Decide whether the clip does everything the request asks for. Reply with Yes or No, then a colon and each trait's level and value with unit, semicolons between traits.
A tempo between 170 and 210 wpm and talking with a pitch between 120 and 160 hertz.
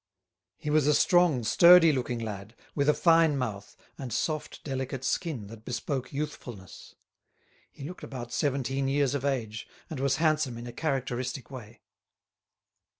No: average, 150 wpm; low, 135 Hz